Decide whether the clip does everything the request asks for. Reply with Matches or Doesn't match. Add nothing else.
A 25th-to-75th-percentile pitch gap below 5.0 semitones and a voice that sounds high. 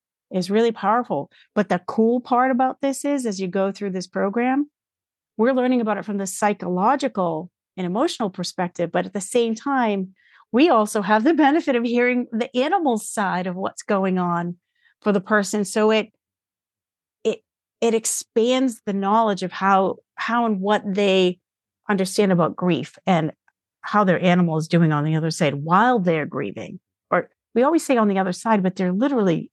Matches